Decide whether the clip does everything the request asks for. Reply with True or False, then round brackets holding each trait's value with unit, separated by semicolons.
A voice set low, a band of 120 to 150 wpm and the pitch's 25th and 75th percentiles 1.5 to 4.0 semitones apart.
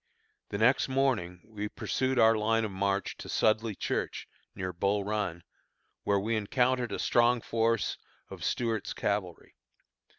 True (110 Hz; 140 wpm; 2.6 semitones)